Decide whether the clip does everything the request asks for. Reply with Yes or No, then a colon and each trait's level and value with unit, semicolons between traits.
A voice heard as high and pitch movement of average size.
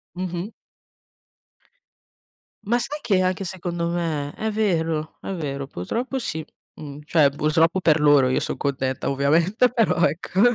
No: medium, 165 Hz; average, 4.4 semitones